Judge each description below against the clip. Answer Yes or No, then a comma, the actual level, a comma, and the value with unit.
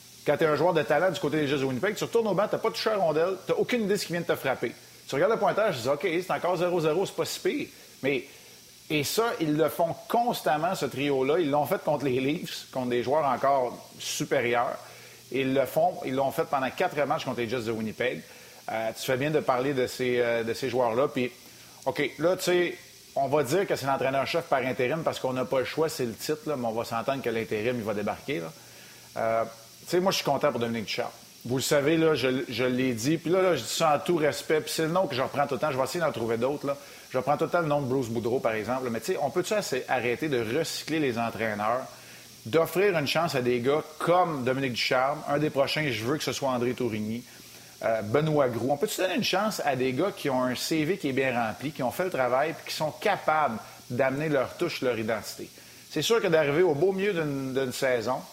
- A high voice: No, medium, 140 Hz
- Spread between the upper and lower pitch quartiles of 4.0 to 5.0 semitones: Yes, average, 4.3 semitones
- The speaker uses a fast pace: Yes, fast, 260 wpm